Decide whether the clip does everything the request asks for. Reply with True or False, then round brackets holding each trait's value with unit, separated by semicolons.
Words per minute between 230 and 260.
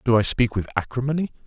False (205 wpm)